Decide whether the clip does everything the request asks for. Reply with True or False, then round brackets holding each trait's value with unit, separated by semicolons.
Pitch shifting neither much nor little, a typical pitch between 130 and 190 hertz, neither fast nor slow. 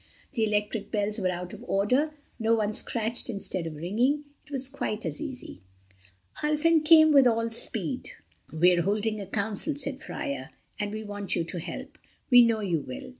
False (5.0 semitones; 215 Hz; 175 wpm)